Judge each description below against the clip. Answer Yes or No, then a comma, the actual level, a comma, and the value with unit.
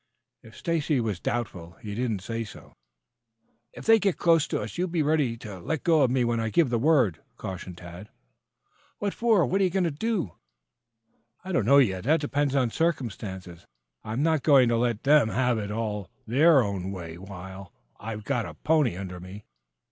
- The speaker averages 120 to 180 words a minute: No, average, 195 wpm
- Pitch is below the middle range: Yes, low, 120 Hz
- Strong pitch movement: Yes, wide, 7.2 semitones